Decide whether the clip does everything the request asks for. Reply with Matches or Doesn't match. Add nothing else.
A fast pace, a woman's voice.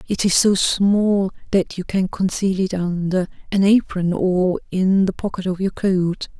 Doesn't match